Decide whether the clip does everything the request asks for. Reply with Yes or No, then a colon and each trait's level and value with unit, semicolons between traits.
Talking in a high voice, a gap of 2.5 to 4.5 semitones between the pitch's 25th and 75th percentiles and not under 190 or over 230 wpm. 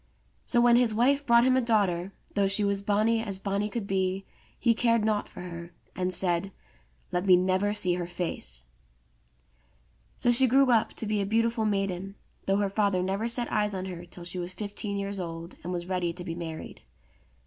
Yes: high, 200 Hz; average, 3.5 semitones; average, 200 wpm